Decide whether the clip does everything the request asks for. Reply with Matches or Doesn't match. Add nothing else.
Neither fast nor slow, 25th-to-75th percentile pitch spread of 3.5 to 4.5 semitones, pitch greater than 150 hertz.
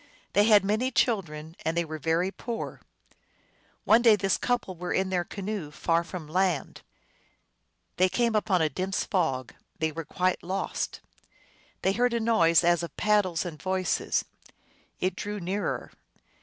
Matches